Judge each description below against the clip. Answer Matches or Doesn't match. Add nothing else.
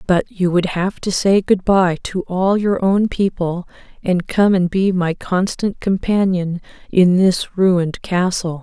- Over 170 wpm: Doesn't match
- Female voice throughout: Matches